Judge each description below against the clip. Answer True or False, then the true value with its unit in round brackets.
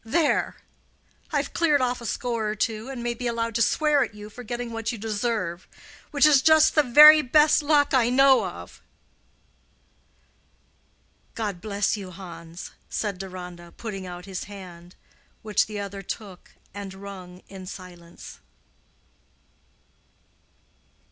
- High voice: True (215 Hz)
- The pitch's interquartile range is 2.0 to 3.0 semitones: False (4.8 semitones)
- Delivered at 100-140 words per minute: True (135 wpm)